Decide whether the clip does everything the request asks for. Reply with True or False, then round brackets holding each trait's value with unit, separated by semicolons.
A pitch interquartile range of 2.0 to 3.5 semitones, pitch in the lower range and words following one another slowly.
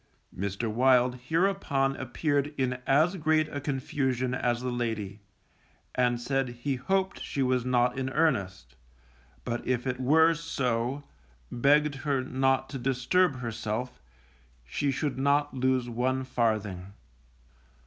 True (2.9 semitones; 130 Hz; 130 wpm)